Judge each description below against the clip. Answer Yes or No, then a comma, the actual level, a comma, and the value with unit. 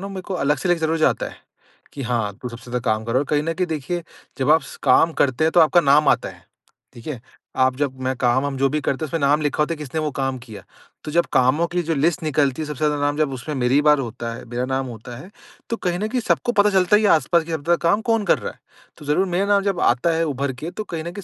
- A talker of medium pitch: Yes, medium, 150 Hz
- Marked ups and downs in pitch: No, average, 4.6 semitones